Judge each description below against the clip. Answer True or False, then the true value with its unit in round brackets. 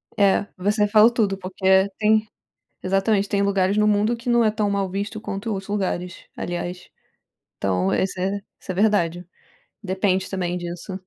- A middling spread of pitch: False (2.2 semitones)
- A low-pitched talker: False (195 Hz)